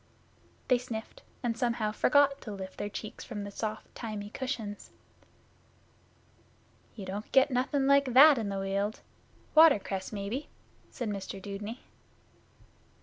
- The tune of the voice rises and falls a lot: No, average, 4.1 semitones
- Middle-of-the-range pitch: No, high, 220 Hz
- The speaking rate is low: Yes, slow, 130 wpm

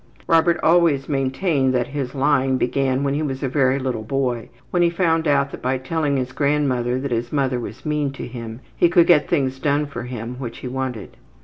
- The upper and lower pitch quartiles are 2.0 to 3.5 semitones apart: Yes, narrow, 2.6 semitones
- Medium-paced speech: No, fast, 210 wpm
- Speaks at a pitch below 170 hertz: Yes, low, 135 Hz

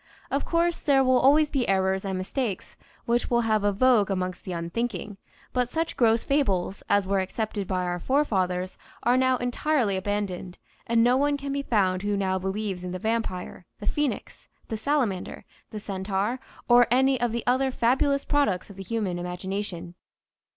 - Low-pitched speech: No, high, 215 Hz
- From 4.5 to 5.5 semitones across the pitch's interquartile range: Yes, average, 5.2 semitones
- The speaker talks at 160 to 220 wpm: Yes, average, 175 wpm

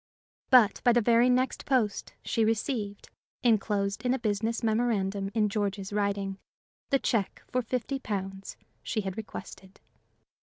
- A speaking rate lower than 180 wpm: Yes, slow, 135 wpm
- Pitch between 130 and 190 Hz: No, high, 215 Hz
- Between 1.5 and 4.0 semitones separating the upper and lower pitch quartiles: Yes, average, 3.2 semitones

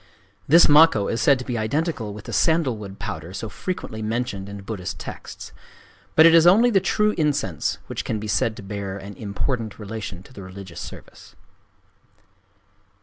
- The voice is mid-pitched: No, low, 110 Hz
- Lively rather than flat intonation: Yes, wide, 6.8 semitones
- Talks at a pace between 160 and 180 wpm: Yes, average, 170 wpm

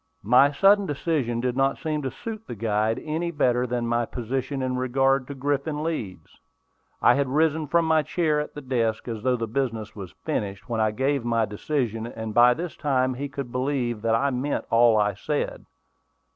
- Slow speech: No, average, 195 wpm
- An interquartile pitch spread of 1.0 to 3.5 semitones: No, average, 4.0 semitones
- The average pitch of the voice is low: Yes, low, 130 Hz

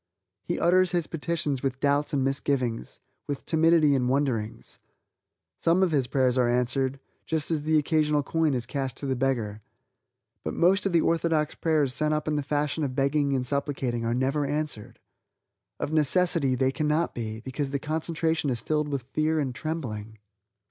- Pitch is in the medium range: Yes, medium, 145 Hz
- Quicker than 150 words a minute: Yes, average, 175 wpm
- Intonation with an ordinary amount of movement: Yes, average, 3.1 semitones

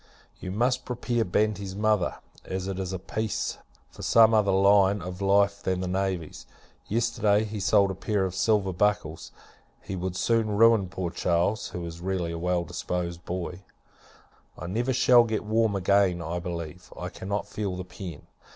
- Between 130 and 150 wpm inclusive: No, average, 170 wpm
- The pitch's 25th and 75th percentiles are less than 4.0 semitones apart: Yes, average, 2.9 semitones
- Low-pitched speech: Yes, very low, 95 Hz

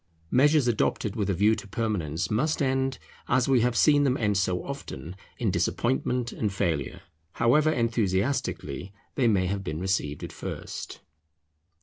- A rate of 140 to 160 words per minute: Yes, average, 150 wpm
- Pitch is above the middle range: No, low, 110 Hz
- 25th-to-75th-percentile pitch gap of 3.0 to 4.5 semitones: No, average, 5.3 semitones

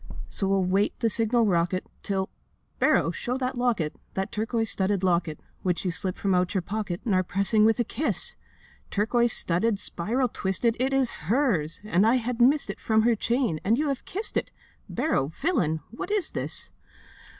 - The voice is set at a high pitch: Yes, high, 215 Hz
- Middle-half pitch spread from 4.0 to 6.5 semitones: Yes, average, 4.7 semitones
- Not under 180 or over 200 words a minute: Yes, average, 185 wpm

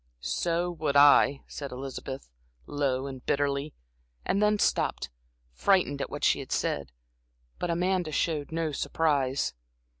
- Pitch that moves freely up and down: No, average, 3.6 semitones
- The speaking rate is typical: No, slow, 130 wpm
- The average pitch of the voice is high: No, medium, 145 Hz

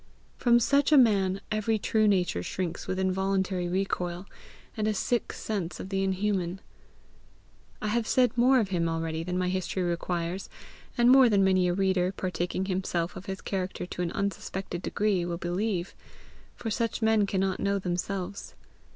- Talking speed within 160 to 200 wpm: Yes, average, 170 wpm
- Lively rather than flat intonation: No, average, 2.8 semitones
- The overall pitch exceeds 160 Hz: Yes, high, 190 Hz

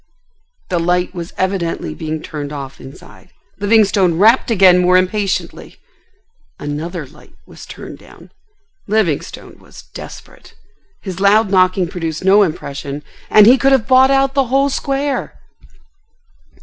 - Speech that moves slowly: Yes, slow, 130 wpm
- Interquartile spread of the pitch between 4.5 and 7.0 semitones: Yes, average, 4.8 semitones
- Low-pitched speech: No, medium, 185 Hz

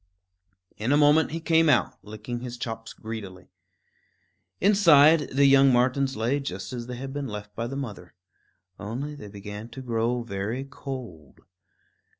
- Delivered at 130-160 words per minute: Yes, average, 150 wpm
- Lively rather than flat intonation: No, average, 4.3 semitones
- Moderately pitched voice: No, low, 125 Hz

